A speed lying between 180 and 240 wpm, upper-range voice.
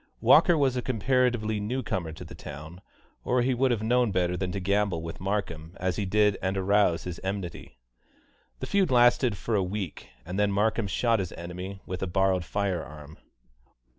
No: average, 190 wpm; low, 100 Hz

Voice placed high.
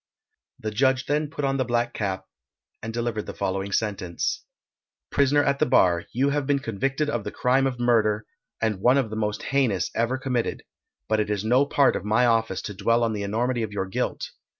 No: low, 115 Hz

